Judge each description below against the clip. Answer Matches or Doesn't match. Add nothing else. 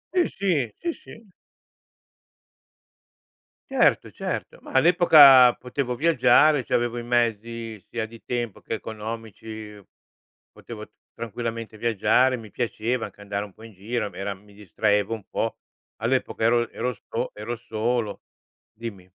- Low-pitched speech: Matches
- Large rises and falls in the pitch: Doesn't match